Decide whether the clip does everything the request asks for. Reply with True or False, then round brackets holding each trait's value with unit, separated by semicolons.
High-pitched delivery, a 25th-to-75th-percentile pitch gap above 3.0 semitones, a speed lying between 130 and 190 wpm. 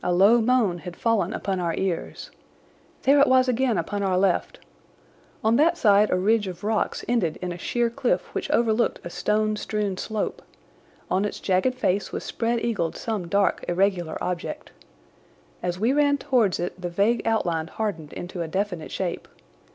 True (205 Hz; 4.5 semitones; 175 wpm)